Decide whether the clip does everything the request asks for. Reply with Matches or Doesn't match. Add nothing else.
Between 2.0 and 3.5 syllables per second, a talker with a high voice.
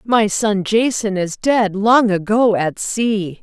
Matches